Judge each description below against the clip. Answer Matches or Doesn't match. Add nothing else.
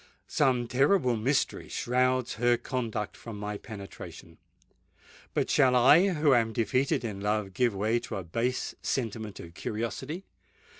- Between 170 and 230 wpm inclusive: Doesn't match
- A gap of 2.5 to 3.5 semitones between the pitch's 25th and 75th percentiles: Matches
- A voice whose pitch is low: Matches